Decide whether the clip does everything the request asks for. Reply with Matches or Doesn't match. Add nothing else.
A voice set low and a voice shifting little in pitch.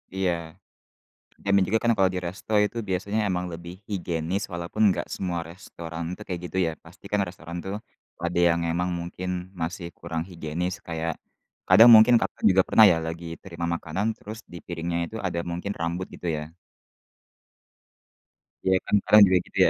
Matches